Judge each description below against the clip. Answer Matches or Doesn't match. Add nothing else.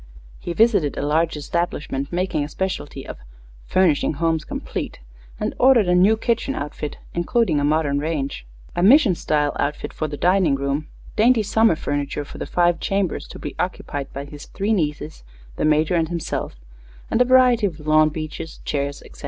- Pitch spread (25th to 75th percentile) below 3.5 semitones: Doesn't match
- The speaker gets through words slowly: Doesn't match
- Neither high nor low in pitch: Matches